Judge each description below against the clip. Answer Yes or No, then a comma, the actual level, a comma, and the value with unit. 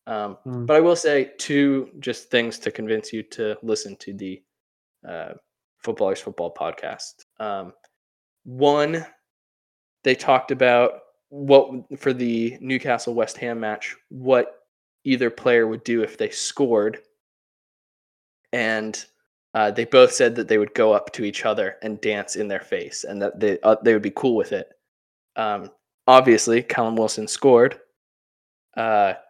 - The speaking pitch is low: Yes, low, 125 Hz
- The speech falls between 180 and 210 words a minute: No, average, 150 wpm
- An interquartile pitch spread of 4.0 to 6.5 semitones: Yes, average, 4.4 semitones